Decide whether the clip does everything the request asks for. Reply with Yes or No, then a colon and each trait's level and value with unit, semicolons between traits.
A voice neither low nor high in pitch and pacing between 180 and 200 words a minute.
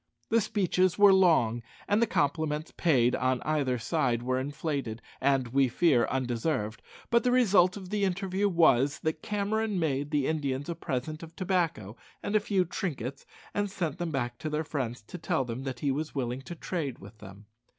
Yes: medium, 155 Hz; average, 185 wpm